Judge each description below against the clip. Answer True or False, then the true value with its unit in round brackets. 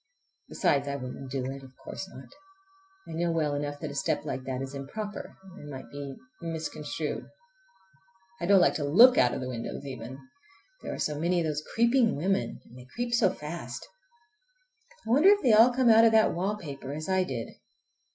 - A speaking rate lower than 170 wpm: False (190 wpm)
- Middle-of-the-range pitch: True (155 Hz)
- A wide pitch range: True (7.7 semitones)